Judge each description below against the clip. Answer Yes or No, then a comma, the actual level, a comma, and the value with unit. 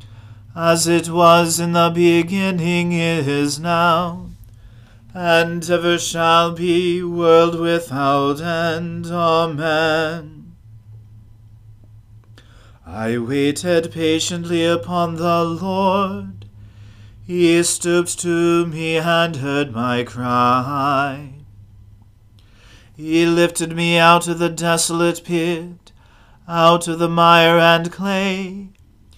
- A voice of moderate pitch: Yes, medium, 165 Hz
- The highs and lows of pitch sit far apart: Yes, wide, 7.3 semitones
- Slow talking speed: Yes, slow, 90 wpm